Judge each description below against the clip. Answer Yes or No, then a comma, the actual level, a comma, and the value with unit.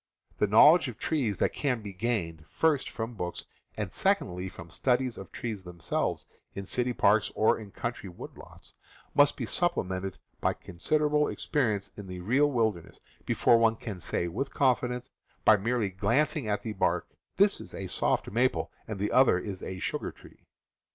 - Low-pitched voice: Yes, low, 110 Hz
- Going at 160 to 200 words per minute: Yes, average, 175 wpm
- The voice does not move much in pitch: No, average, 4.9 semitones